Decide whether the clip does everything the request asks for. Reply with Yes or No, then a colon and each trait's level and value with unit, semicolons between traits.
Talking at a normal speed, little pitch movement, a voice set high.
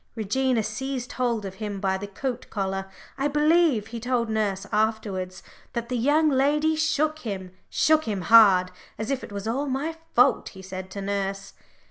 No: average, 175 wpm; wide, 5.4 semitones; high, 225 Hz